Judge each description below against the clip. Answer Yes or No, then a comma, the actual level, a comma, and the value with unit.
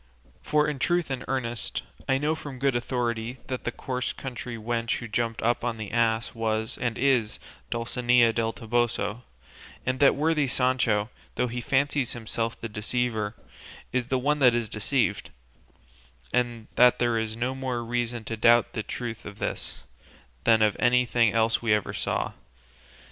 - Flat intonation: Yes, narrow, 2.1 semitones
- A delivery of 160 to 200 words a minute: Yes, average, 165 wpm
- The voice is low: Yes, low, 120 Hz